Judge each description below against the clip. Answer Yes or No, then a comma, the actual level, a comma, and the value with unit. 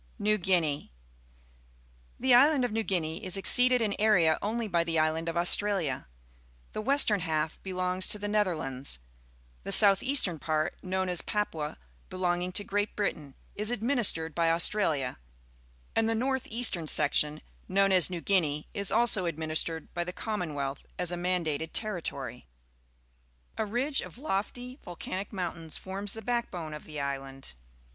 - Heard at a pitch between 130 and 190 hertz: Yes, medium, 185 Hz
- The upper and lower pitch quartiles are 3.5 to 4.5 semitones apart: No, average, 4.9 semitones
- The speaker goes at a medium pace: Yes, average, 155 wpm